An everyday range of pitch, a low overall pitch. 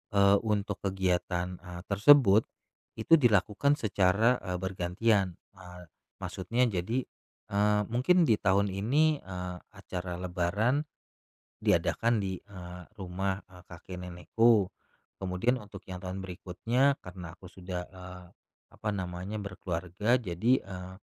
Yes: average, 3.2 semitones; very low, 95 Hz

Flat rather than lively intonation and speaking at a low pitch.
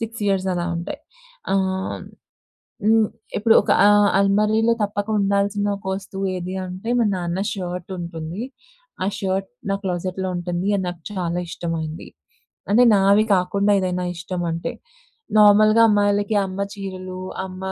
No: narrow, 2.2 semitones; high, 190 Hz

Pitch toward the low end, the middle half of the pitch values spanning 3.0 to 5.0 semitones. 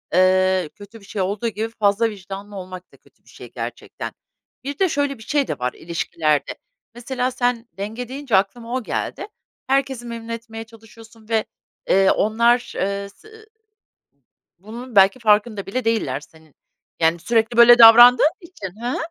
No: high, 225 Hz; average, 3.7 semitones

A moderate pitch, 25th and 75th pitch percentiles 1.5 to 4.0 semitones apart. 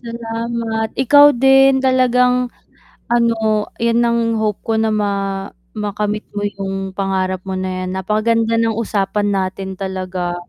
No: high, 215 Hz; average, 3.3 semitones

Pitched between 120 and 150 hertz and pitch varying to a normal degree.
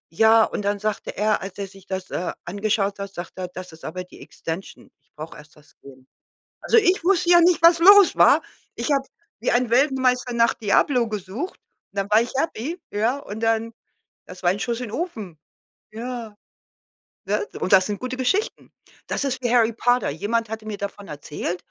No: high, 220 Hz; average, 4.6 semitones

